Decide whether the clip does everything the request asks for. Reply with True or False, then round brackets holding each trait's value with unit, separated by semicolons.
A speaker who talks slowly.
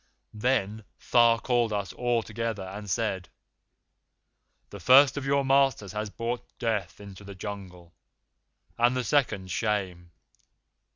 True (125 wpm)